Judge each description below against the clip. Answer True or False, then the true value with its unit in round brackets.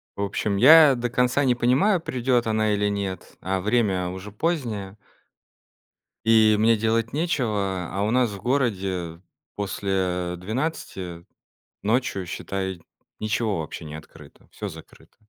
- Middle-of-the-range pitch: False (105 Hz)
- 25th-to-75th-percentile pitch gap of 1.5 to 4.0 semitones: False (4.4 semitones)